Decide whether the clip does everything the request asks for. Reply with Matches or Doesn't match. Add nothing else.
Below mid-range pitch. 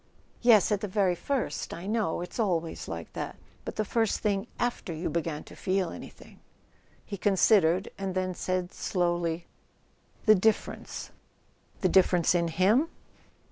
Doesn't match